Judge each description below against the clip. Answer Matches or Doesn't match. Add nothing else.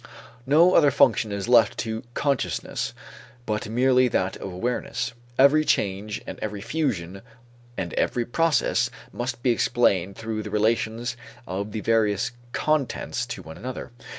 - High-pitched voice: Doesn't match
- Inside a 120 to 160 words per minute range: Matches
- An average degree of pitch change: Matches